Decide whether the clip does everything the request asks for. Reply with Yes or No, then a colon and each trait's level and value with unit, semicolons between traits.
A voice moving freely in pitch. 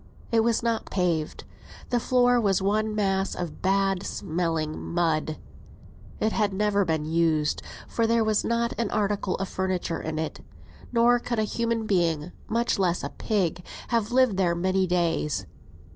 No: average, 4.7 semitones